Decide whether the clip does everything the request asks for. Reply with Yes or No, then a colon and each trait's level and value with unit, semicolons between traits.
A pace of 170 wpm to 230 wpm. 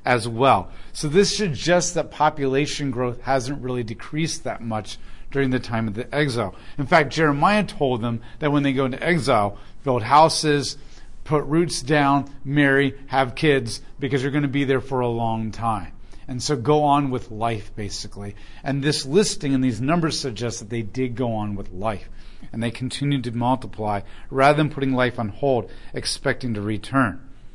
Yes: average, 180 wpm